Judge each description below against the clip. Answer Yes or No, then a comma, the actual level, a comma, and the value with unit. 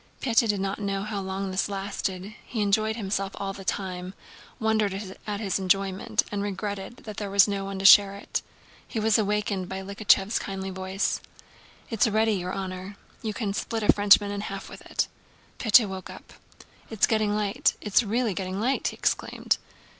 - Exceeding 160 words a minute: Yes, average, 180 wpm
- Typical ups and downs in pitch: No, narrow, 1.7 semitones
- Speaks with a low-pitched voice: No, high, 200 Hz